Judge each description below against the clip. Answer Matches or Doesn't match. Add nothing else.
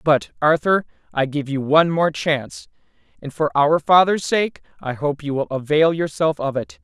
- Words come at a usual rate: Matches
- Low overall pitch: Doesn't match